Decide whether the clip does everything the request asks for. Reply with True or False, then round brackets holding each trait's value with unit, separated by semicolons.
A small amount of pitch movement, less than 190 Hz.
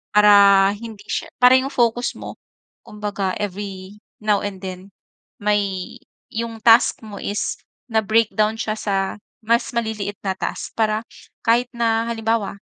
False (2.2 semitones; 215 Hz)